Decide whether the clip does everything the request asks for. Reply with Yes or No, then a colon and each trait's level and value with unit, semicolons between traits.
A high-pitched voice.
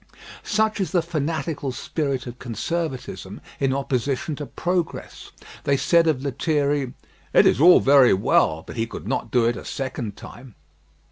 No: medium, 140 Hz